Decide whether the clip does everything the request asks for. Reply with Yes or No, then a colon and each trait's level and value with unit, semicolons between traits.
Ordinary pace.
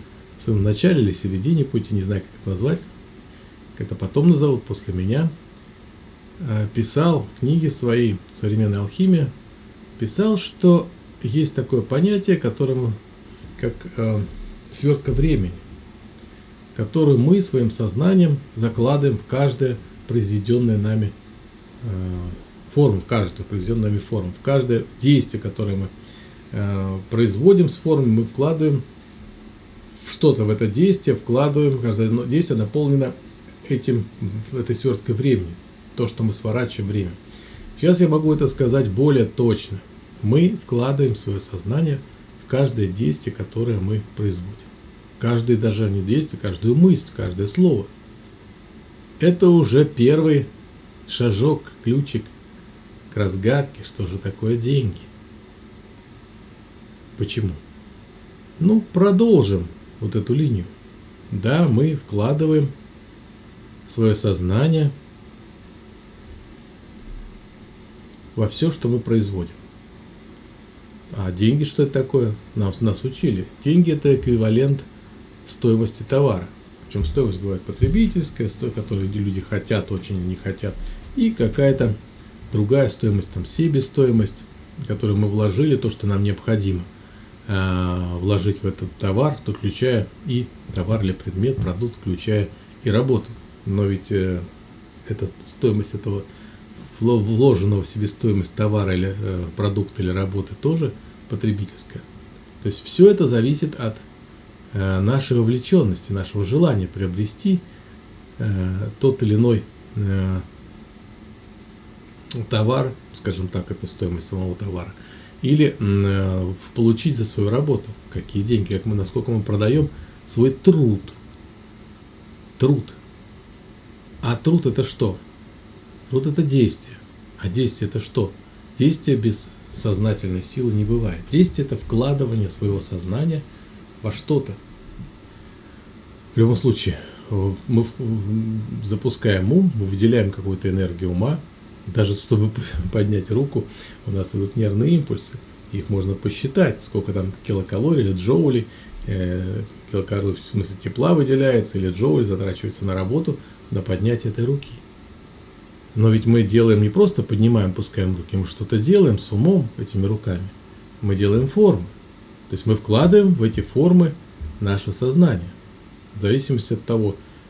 Yes: average, 120 wpm